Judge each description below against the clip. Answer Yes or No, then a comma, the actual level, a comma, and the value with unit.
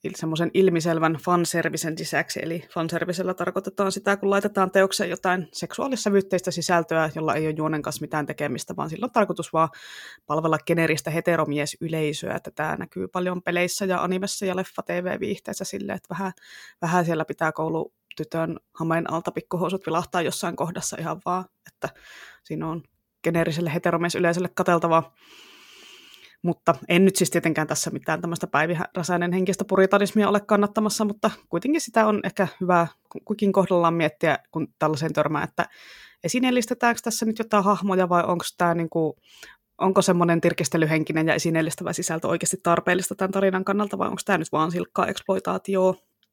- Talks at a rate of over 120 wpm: Yes, average, 150 wpm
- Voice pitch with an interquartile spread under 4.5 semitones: Yes, average, 2.9 semitones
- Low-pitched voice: No, medium, 175 Hz